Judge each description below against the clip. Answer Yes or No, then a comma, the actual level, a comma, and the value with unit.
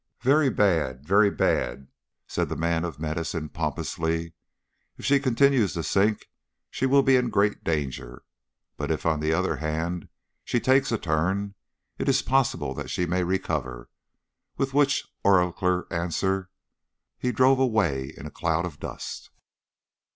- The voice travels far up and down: Yes, wide, 6.8 semitones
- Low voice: Yes, very low, 90 Hz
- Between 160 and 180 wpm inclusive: No, average, 150 wpm